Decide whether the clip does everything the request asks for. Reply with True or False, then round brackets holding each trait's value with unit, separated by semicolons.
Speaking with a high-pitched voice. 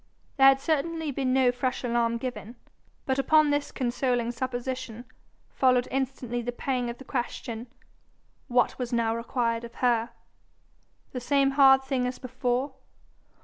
True (255 Hz)